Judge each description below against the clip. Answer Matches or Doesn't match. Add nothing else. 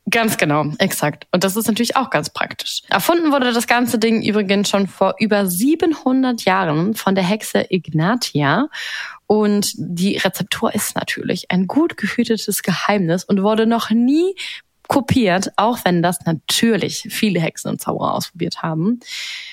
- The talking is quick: Doesn't match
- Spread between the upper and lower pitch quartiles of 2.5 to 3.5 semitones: Doesn't match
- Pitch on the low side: Doesn't match